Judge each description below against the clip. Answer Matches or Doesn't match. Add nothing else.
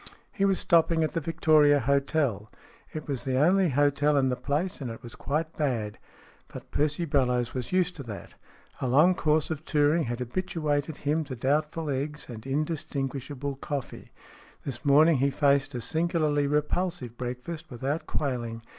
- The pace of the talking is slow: Doesn't match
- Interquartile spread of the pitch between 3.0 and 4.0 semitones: Matches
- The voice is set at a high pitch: Doesn't match